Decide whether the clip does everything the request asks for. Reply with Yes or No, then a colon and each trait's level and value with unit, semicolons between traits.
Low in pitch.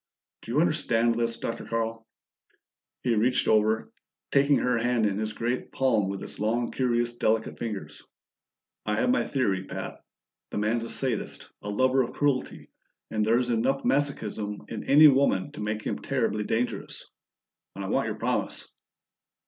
Yes: low, 115 Hz